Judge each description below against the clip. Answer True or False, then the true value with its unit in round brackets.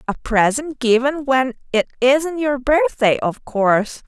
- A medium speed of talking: True (145 wpm)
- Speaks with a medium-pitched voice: False (260 Hz)